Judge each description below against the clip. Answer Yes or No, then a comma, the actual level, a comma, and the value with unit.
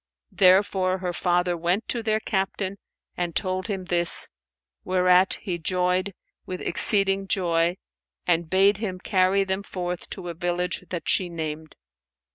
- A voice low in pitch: No, medium, 185 Hz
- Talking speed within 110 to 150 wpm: Yes, average, 140 wpm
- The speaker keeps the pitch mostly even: Yes, narrow, 1.6 semitones